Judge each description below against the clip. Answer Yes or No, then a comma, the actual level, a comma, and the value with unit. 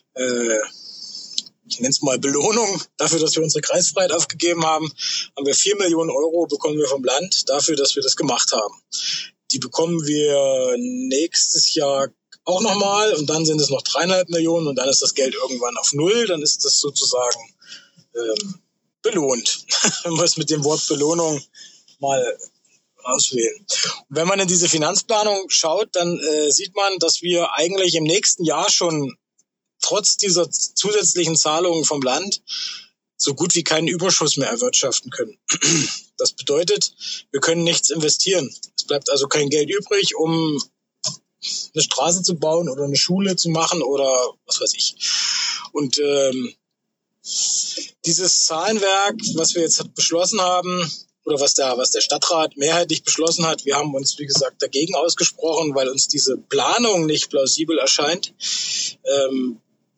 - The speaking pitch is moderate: Yes, medium, 165 Hz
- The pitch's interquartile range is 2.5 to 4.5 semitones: No, average, 5.0 semitones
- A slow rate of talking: No, average, 155 wpm